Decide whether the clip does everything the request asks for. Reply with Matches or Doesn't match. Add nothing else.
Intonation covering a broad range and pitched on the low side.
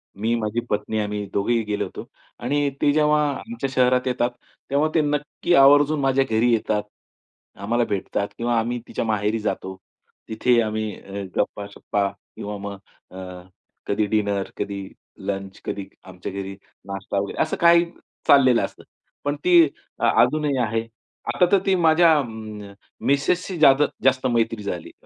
Matches